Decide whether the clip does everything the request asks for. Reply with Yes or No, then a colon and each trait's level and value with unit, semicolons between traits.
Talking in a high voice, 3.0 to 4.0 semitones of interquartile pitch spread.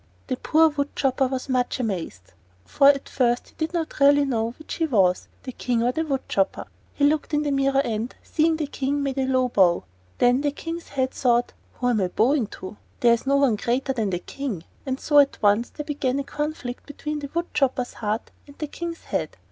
Yes: very high, 265 Hz; average, 3.3 semitones